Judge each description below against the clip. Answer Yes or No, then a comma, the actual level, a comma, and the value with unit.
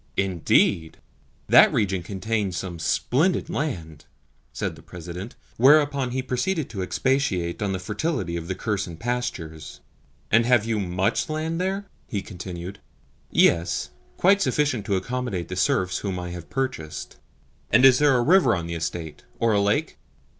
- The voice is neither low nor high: No, low, 105 Hz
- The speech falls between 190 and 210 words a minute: No, average, 155 wpm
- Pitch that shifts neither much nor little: No, wide, 6.7 semitones